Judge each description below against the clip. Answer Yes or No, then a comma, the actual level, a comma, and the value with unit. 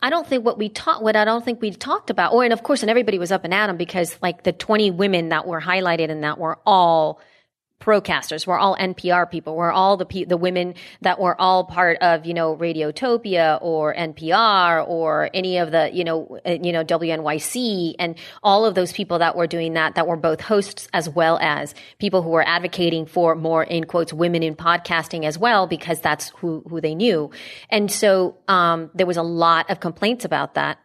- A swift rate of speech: Yes, fast, 220 wpm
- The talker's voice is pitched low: No, medium, 175 Hz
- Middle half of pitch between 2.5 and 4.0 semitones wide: Yes, average, 2.9 semitones